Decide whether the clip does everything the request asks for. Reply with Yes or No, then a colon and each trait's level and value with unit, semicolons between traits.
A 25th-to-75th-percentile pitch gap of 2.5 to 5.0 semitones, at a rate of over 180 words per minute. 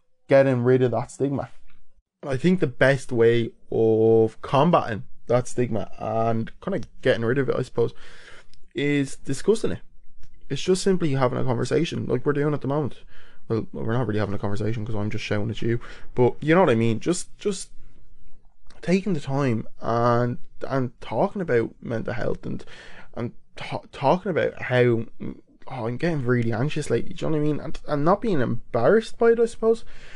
Yes: average, 4.7 semitones; average, 190 wpm